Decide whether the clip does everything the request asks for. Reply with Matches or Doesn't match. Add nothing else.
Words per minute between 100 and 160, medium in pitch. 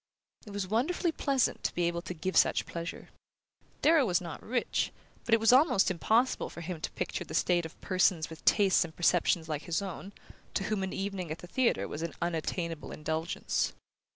Doesn't match